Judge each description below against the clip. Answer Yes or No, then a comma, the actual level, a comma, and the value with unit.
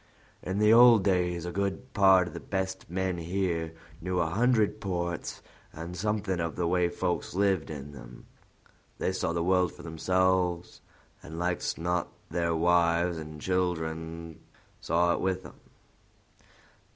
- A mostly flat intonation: Yes, narrow, 2.1 semitones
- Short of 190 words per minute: Yes, average, 150 wpm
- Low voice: Yes, very low, 90 Hz